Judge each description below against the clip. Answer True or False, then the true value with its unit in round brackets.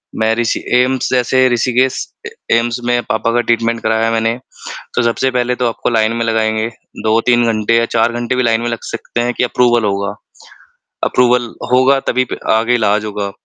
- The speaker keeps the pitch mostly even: True (1.7 semitones)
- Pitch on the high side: False (115 Hz)